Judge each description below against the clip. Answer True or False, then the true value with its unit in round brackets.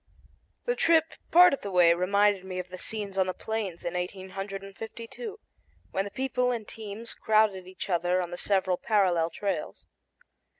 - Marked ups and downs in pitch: False (3.3 semitones)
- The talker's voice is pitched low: False (195 Hz)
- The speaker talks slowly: False (165 wpm)